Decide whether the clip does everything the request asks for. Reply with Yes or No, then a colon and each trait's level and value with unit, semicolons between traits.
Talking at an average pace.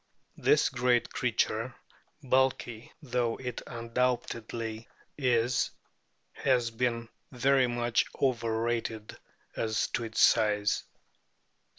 No: slow, 90 wpm